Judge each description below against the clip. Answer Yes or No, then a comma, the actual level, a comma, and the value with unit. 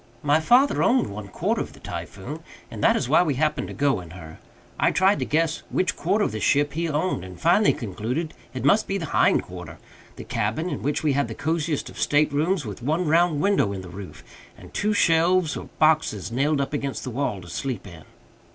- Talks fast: Yes, fast, 225 wpm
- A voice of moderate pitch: Yes, medium, 150 Hz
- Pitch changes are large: Yes, wide, 6.4 semitones